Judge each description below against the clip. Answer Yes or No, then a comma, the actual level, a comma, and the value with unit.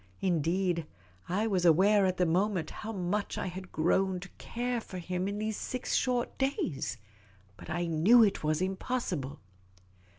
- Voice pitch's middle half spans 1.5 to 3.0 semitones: No, average, 3.4 semitones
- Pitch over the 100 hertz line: Yes, medium, 185 Hz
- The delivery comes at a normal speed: Yes, average, 160 wpm